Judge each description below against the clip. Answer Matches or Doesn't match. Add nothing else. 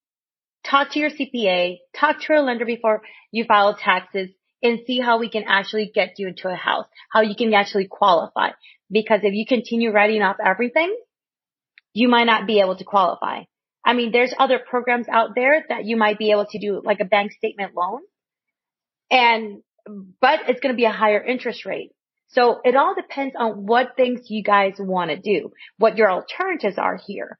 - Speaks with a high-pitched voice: Matches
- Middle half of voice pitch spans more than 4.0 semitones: Doesn't match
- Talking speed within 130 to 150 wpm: Doesn't match